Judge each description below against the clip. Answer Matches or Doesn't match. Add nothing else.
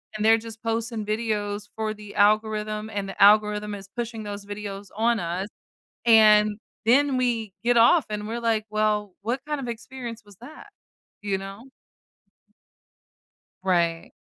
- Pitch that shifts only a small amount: Matches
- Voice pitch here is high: Matches